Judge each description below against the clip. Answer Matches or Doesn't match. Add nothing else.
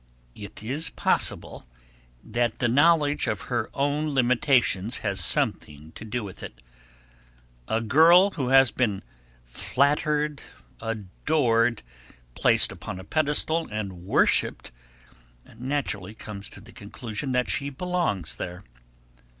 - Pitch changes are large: Matches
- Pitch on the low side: Matches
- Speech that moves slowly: Matches